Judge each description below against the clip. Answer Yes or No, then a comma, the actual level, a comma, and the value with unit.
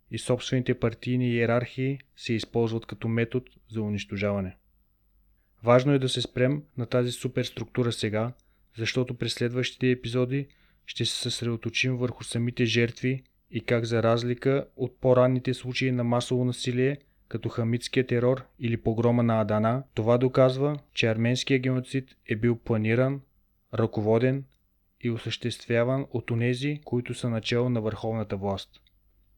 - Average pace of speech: Yes, average, 135 wpm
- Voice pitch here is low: Yes, low, 120 Hz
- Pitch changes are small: Yes, narrow, 2.0 semitones